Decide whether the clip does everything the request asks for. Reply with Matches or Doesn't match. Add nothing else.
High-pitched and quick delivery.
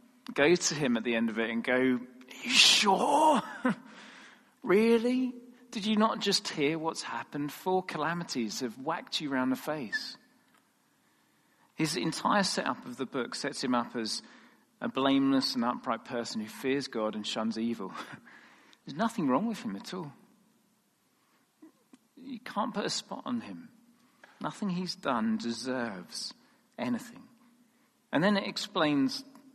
Doesn't match